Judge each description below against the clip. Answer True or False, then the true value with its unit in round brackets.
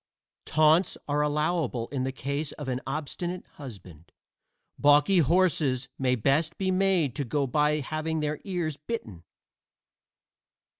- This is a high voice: False (150 Hz)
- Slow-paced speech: True (130 wpm)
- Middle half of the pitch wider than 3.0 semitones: True (3.4 semitones)